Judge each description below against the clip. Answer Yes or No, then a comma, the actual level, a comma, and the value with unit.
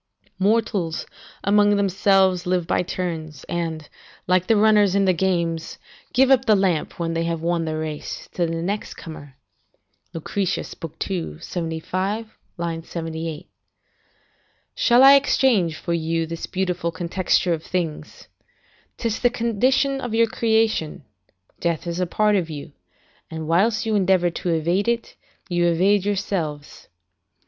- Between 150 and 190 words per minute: No, average, 140 wpm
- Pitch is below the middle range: No, medium, 180 Hz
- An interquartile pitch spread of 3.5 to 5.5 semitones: Yes, average, 3.9 semitones